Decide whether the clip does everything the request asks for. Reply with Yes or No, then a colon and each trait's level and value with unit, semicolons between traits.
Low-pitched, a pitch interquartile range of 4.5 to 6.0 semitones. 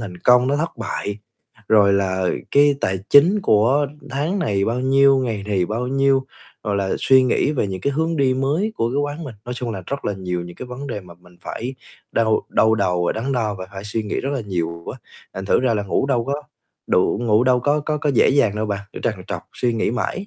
Yes: low, 120 Hz; wide, 5.4 semitones